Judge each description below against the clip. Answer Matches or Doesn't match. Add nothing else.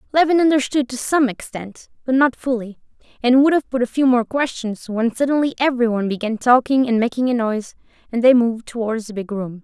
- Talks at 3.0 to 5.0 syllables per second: Doesn't match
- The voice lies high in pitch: Matches